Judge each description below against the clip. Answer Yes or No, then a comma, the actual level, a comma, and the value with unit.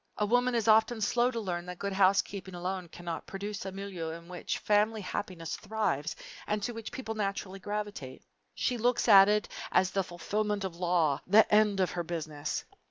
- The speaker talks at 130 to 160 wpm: No, average, 190 wpm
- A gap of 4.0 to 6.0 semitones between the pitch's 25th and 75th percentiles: No, average, 3.2 semitones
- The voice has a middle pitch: No, high, 195 Hz